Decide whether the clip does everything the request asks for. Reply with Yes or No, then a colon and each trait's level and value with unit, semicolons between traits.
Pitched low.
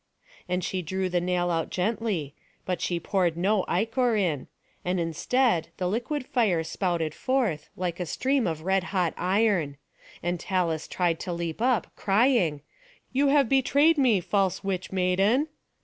No: medium, 185 Hz